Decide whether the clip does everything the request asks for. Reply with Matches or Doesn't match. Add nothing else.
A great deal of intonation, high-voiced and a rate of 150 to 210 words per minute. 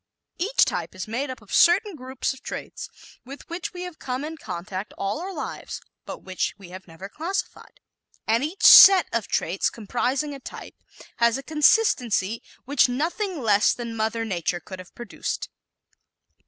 Matches